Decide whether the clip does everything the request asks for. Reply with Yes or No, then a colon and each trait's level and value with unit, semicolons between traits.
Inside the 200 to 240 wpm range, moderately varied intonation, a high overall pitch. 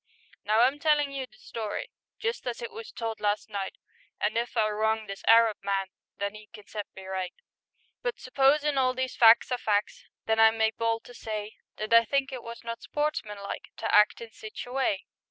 Yes: fast, 205 wpm; average, 3.6 semitones; high, 225 Hz